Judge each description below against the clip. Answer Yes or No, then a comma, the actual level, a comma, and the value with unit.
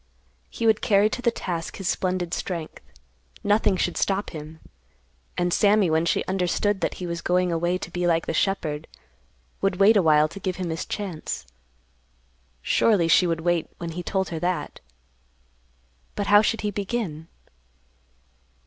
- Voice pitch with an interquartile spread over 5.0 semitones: No, average, 3.2 semitones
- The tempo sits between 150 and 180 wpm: Yes, average, 160 wpm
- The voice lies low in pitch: No, medium, 180 Hz